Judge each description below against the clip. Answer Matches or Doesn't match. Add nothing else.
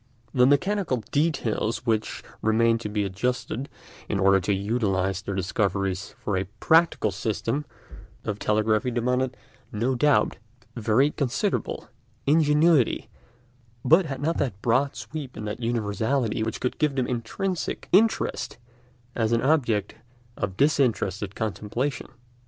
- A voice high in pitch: Doesn't match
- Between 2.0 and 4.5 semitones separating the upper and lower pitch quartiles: Doesn't match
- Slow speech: Matches